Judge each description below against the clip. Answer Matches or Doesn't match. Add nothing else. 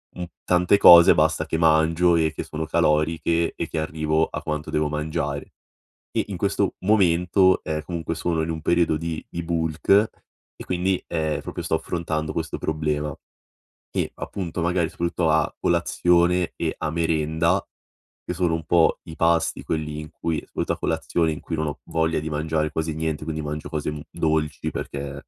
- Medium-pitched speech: Doesn't match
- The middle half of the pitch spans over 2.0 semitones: Doesn't match